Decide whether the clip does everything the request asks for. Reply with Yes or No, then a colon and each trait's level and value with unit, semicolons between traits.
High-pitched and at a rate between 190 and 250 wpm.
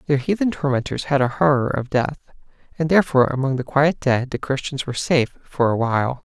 No: low, 135 Hz; average, 200 wpm